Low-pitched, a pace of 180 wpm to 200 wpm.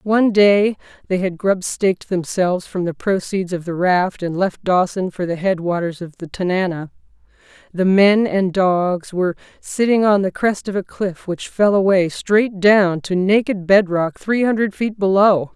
No: high, 190 Hz; average, 185 wpm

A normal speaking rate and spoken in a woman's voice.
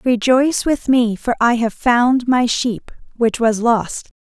Yes: average, 170 wpm; female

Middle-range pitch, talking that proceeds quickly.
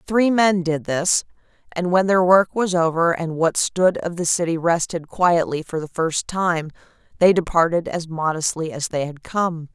No: medium, 170 Hz; average, 185 wpm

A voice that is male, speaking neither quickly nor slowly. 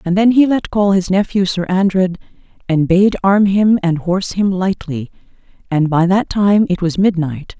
No: female; average, 190 wpm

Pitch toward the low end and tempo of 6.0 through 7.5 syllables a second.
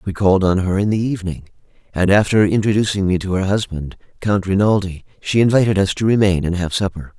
Yes: low, 100 Hz; 6.1 syllables/s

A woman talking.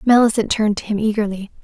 Yes: female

